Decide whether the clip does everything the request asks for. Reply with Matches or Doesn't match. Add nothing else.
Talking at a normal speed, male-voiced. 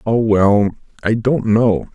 Matches